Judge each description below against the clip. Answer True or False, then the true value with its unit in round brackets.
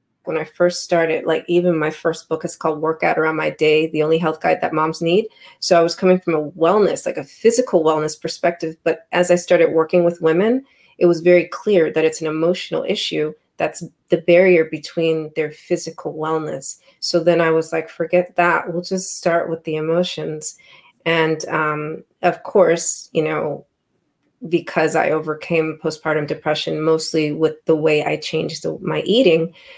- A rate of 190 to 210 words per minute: False (180 wpm)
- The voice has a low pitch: False (165 Hz)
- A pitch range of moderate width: False (1.8 semitones)